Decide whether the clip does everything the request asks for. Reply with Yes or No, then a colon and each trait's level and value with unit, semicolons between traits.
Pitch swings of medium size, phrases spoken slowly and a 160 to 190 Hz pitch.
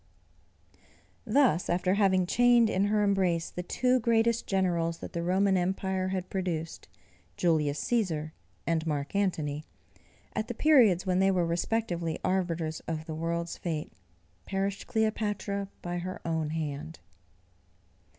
Yes: average, 3.4 semitones; slow, 130 wpm; medium, 185 Hz